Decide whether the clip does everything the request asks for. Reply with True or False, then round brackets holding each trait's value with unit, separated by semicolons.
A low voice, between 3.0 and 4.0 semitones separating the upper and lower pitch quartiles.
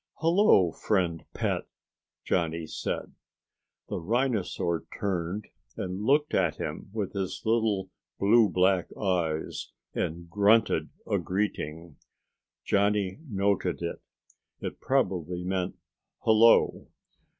True (95 Hz; 3.6 semitones)